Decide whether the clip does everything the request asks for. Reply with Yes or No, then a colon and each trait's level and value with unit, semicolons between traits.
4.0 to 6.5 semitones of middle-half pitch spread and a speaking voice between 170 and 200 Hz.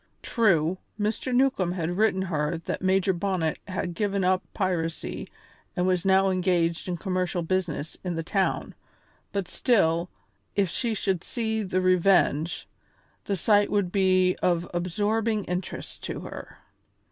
No: narrow, 2.4 semitones; medium, 185 Hz